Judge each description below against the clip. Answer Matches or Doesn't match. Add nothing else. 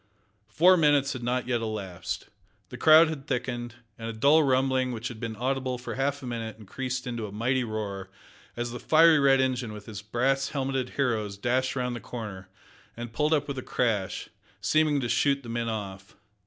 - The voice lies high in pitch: Doesn't match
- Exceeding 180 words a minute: Matches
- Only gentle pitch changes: Doesn't match